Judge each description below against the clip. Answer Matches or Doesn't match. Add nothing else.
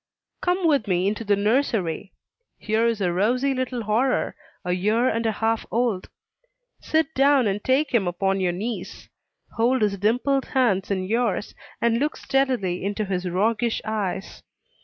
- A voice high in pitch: Matches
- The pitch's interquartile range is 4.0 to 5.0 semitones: Matches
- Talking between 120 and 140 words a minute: Doesn't match